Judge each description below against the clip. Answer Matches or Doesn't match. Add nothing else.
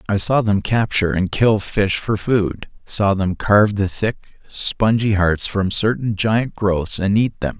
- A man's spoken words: Matches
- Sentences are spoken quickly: Doesn't match